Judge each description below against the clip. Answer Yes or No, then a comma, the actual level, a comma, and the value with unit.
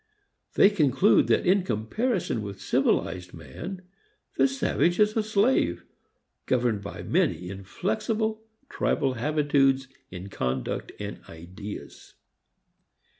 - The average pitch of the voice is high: No, low, 135 Hz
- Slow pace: Yes, slow, 105 wpm